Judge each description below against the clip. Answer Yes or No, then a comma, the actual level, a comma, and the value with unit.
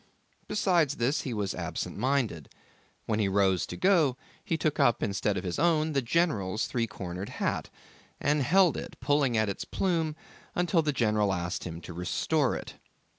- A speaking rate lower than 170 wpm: No, average, 175 wpm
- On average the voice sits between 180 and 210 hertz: No, low, 125 Hz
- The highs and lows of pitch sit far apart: Yes, wide, 7.5 semitones